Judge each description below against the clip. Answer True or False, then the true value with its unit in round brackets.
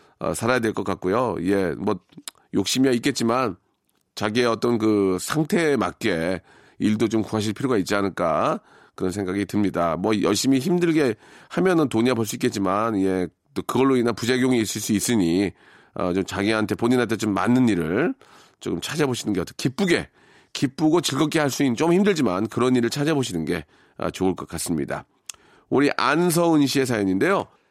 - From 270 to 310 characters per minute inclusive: False (350 characters per minute)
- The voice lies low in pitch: True (115 Hz)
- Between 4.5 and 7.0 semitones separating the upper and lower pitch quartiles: True (5.5 semitones)